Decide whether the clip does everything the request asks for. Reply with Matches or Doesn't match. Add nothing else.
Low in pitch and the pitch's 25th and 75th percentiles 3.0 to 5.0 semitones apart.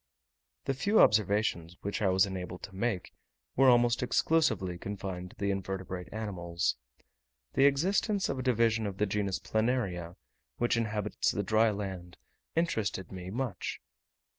Matches